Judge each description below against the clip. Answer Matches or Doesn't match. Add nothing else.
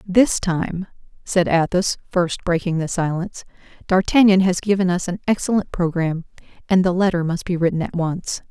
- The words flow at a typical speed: Matches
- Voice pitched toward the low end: Doesn't match